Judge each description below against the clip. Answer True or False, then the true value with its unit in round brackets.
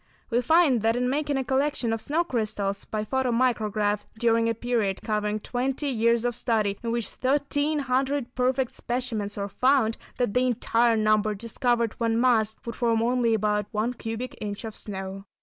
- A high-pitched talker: True (235 Hz)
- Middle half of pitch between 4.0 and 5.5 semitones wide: False (3.0 semitones)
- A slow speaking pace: False (175 wpm)